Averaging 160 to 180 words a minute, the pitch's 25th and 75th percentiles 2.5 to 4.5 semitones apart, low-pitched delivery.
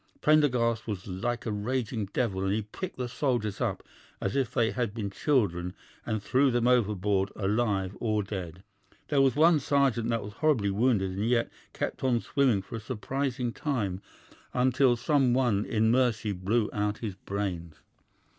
Yes: average, 165 wpm; average, 4.0 semitones; low, 115 Hz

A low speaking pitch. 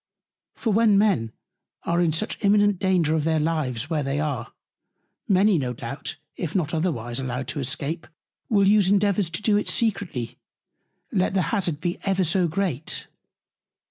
No: medium, 170 Hz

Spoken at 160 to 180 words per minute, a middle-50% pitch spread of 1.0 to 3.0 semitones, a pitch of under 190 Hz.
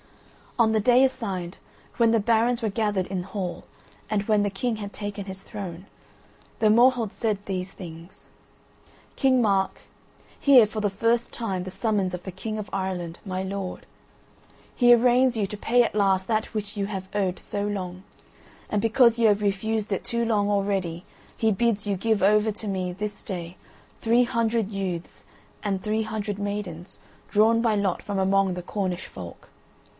No: average, 175 wpm; average, 2.7 semitones; high, 205 Hz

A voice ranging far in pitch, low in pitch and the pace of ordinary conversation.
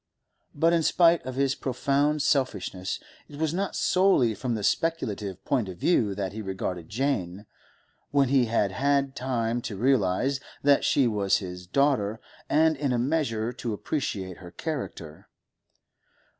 Yes: wide, 6.0 semitones; low, 125 Hz; average, 150 wpm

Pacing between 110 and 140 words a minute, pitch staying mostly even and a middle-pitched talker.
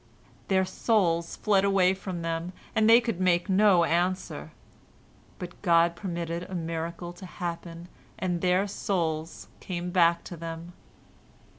Yes: slow, 135 wpm; narrow, 2.0 semitones; medium, 175 Hz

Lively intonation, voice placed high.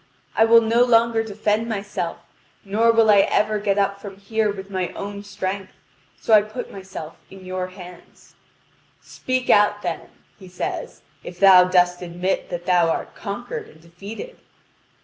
No: average, 3.0 semitones; high, 200 Hz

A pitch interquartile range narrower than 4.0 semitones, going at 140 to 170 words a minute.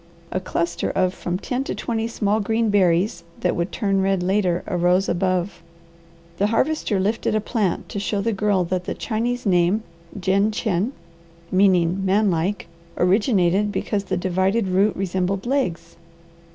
Yes: average, 2.8 semitones; average, 150 wpm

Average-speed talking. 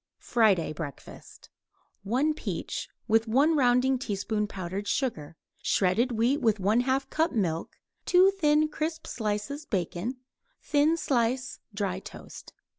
No: slow, 115 wpm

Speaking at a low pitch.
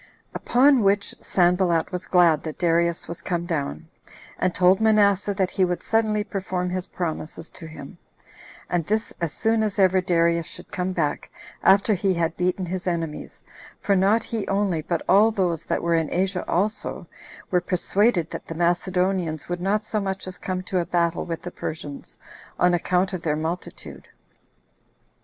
No: medium, 180 Hz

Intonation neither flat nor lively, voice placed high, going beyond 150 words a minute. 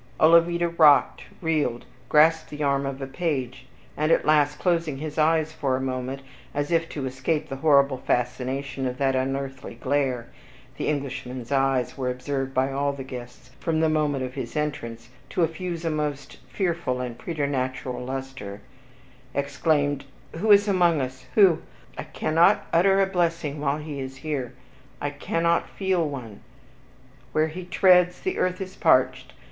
No: average, 3.7 semitones; medium, 145 Hz; average, 160 wpm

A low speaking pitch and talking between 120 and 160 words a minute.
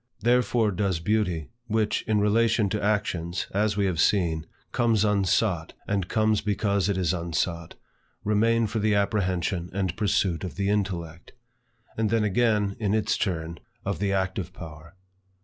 Yes: low, 100 Hz; average, 150 wpm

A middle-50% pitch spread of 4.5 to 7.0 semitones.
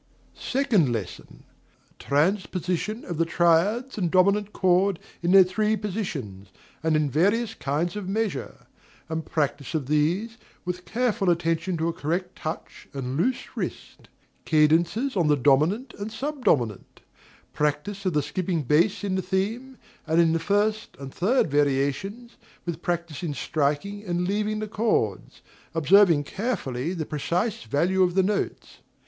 Yes: average, 5.2 semitones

